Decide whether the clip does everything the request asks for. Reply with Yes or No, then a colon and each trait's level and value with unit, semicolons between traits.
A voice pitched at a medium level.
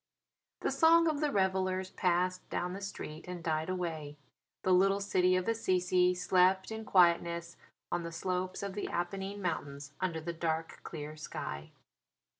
Yes: medium, 180 Hz